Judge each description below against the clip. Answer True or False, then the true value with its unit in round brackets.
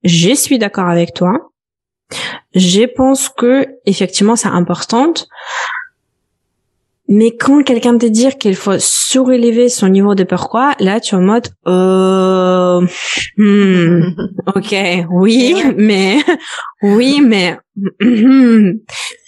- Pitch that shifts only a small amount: False (5.4 semitones)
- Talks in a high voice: True (210 Hz)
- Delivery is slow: True (110 wpm)